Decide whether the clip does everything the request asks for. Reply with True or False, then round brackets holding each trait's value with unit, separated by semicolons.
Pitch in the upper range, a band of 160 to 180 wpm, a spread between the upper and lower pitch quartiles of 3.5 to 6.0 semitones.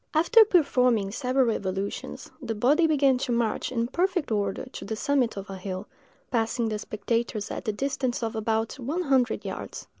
True (235 Hz; 175 wpm; 4.1 semitones)